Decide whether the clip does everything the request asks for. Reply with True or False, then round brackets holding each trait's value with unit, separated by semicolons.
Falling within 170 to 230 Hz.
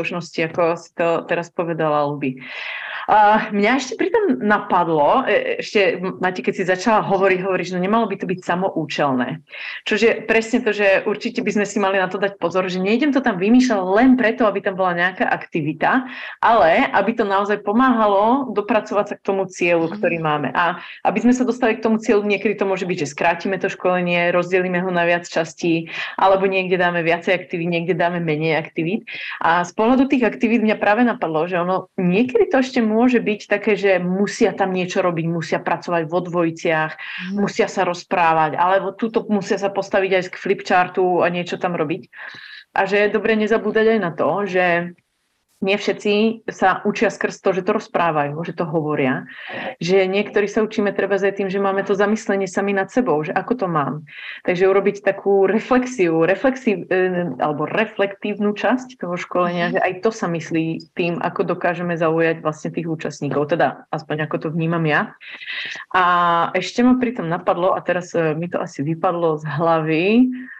True (190 Hz)